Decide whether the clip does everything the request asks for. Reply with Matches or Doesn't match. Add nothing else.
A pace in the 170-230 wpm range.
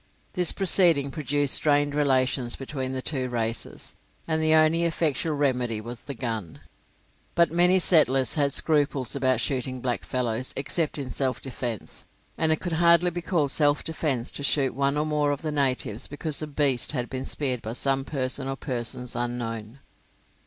Matches